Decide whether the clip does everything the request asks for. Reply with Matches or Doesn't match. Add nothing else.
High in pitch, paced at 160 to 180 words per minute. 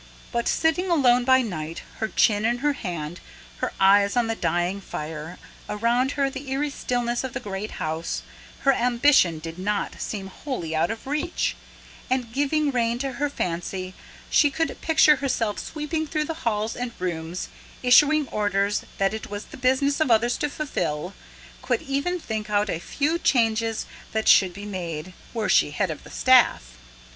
Matches